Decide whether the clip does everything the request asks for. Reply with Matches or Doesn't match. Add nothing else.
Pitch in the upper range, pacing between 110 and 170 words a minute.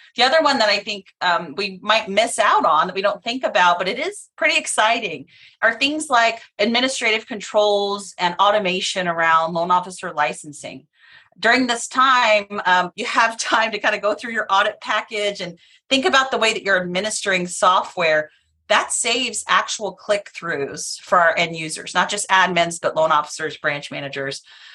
Doesn't match